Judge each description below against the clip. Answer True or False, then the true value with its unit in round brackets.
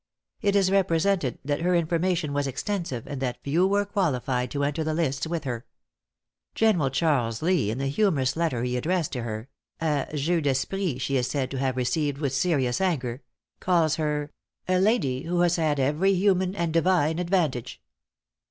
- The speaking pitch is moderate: True (155 Hz)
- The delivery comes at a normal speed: True (175 wpm)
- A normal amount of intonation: True (5.0 semitones)